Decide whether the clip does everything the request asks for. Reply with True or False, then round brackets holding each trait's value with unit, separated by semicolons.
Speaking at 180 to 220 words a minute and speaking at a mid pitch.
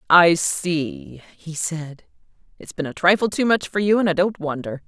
True (195 wpm; 175 Hz)